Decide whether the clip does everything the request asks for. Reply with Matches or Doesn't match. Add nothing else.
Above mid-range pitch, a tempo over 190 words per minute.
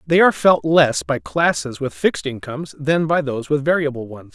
Doesn't match